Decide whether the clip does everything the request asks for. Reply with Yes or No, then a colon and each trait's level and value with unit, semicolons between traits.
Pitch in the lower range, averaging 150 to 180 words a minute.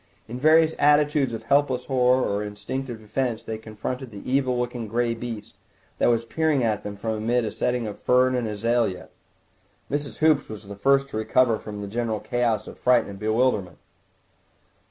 Yes: low, 120 Hz; average, 175 wpm